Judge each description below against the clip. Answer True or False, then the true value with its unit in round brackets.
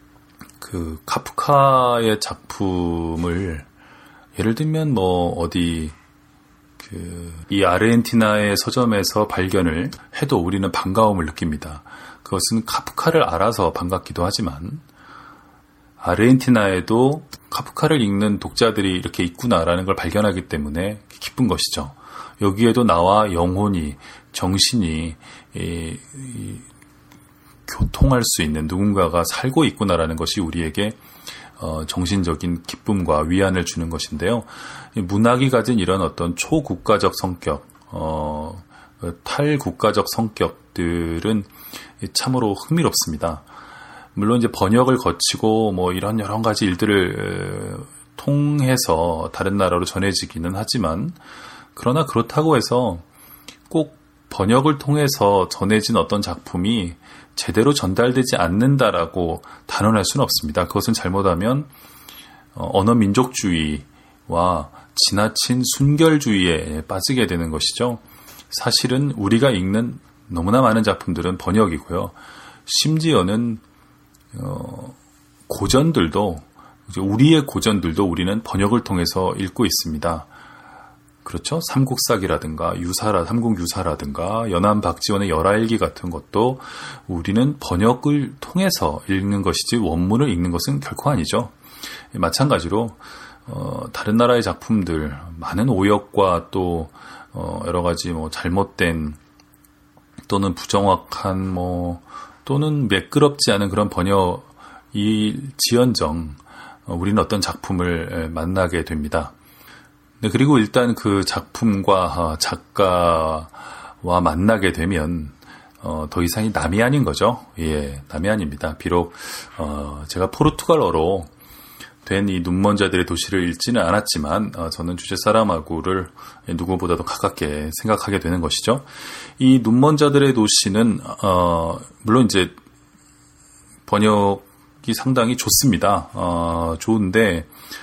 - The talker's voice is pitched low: True (95 Hz)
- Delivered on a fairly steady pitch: False (5.3 semitones)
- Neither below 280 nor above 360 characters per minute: False (260 characters per minute)